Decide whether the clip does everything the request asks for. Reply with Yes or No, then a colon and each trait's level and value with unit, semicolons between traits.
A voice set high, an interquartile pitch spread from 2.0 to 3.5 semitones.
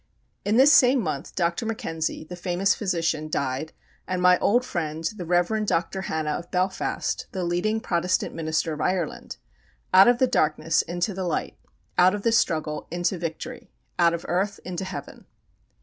No: medium, 175 Hz; average, 3.1 semitones